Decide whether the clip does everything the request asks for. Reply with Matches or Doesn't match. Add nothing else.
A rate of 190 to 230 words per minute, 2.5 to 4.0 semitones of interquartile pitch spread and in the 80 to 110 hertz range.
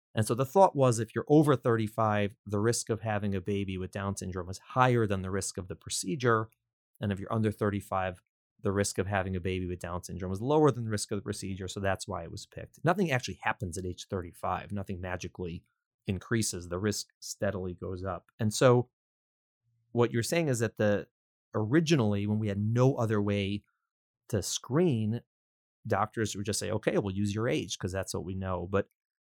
Matches